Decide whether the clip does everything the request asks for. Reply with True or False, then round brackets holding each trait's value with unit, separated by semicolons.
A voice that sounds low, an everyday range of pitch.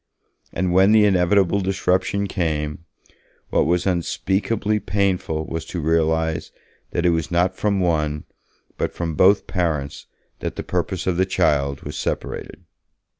True (90 Hz; 3.0 semitones)